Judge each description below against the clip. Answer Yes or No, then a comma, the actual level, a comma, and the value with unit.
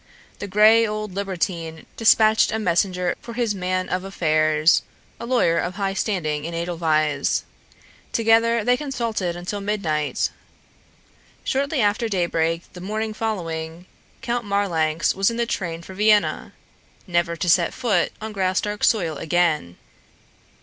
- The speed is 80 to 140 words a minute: Yes, slow, 135 wpm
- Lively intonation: No, average, 4.3 semitones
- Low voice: No, high, 190 Hz